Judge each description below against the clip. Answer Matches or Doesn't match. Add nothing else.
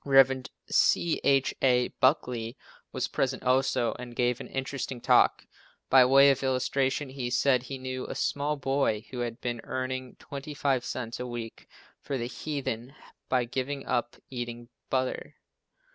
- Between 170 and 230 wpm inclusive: Doesn't match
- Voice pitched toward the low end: Matches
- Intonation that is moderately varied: Doesn't match